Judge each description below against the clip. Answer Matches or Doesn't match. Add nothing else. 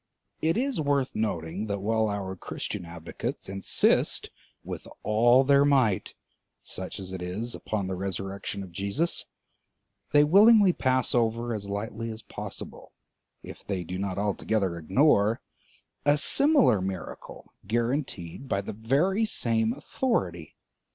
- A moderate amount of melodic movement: Doesn't match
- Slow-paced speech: Matches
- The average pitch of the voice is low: Matches